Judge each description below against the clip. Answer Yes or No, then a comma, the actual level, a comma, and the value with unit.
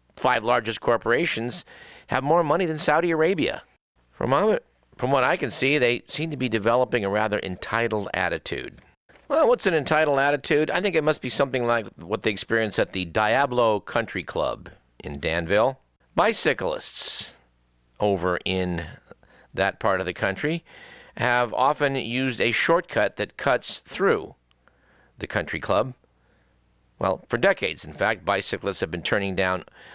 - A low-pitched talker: Yes, low, 115 Hz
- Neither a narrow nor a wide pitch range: No, wide, 7.3 semitones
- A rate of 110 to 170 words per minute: Yes, average, 150 wpm